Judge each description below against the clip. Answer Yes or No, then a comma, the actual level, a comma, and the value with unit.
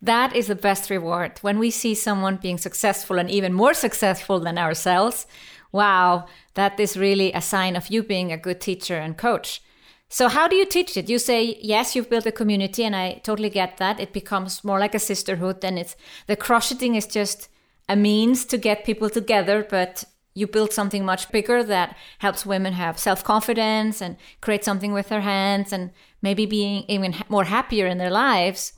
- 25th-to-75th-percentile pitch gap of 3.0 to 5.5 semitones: No, narrow, 2.5 semitones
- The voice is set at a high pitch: Yes, high, 200 Hz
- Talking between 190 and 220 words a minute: Yes, average, 195 wpm